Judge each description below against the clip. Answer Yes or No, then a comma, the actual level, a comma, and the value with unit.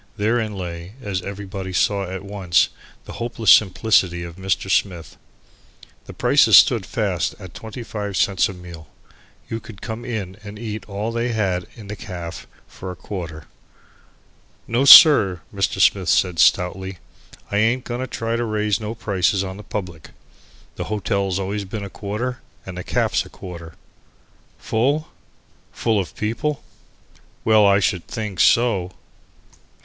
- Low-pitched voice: Yes, low, 100 Hz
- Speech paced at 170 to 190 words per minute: No, average, 150 wpm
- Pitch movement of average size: Yes, average, 3.3 semitones